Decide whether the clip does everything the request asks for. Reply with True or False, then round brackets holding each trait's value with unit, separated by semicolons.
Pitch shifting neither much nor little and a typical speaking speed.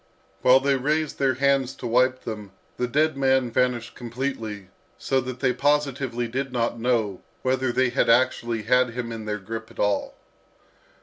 False (2.3 semitones; 170 wpm)